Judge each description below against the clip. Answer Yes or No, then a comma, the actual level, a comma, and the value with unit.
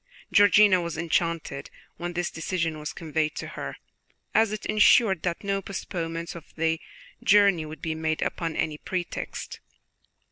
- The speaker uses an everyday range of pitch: Yes, average, 3.3 semitones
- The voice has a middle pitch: Yes, medium, 170 Hz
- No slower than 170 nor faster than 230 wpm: No, average, 145 wpm